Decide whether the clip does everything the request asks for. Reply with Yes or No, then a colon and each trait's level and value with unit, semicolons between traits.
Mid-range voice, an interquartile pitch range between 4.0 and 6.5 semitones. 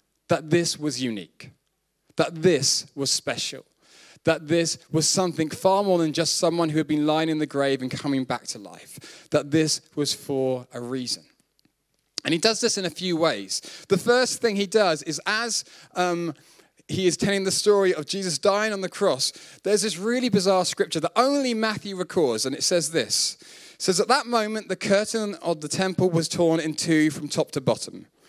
Yes: medium, 170 Hz; average, 4.5 semitones